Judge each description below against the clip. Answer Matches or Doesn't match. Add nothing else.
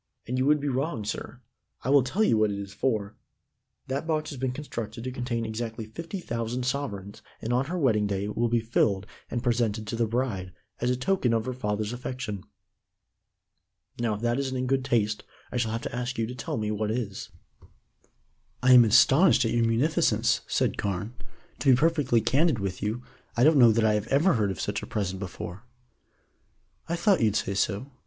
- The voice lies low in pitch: Matches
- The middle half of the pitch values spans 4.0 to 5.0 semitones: Doesn't match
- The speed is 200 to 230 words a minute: Matches